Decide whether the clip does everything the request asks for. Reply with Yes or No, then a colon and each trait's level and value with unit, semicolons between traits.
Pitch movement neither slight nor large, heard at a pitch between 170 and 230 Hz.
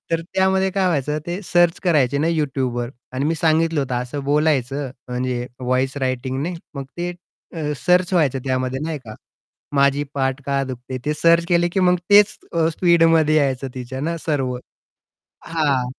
No: average, 4.2 semitones; medium, 145 Hz